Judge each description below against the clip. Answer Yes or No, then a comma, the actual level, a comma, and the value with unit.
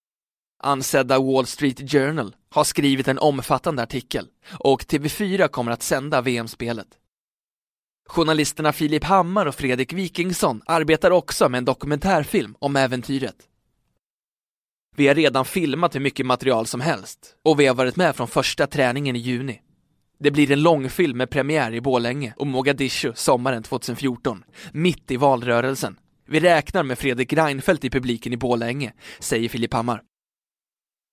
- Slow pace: No, average, 145 wpm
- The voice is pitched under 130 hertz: No, low, 135 Hz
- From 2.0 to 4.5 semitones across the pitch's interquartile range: Yes, average, 3.3 semitones